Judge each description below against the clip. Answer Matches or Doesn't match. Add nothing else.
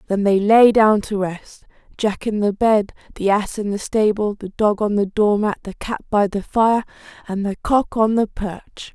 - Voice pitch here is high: Matches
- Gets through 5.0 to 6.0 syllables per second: Doesn't match